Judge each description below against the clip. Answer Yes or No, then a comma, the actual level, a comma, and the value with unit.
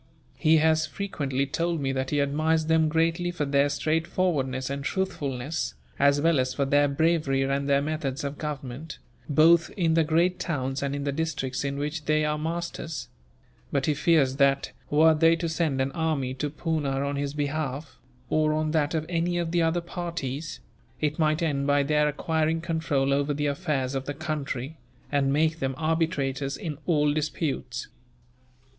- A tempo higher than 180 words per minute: No, average, 175 wpm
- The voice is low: No, medium, 150 Hz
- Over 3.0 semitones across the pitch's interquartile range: No, average, 2.7 semitones